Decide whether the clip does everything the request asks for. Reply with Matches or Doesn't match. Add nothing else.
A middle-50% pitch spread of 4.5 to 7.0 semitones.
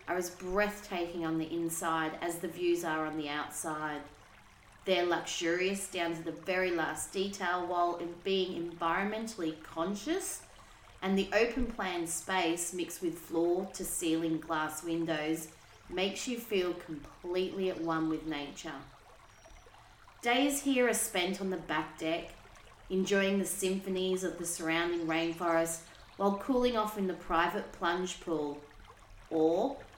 Doesn't match